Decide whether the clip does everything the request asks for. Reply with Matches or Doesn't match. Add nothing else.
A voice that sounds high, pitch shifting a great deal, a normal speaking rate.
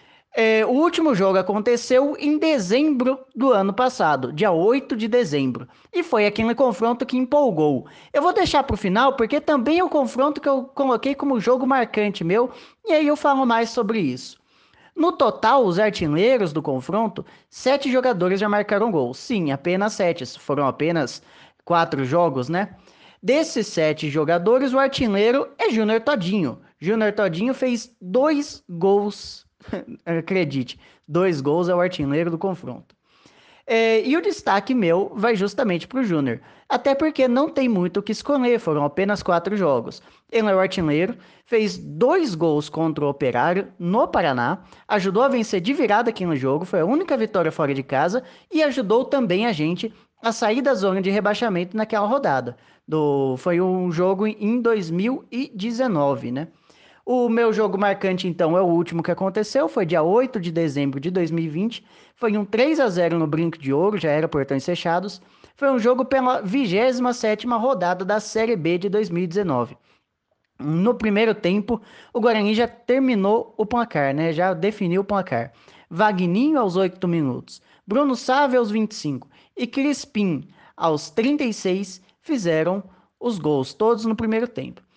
Matches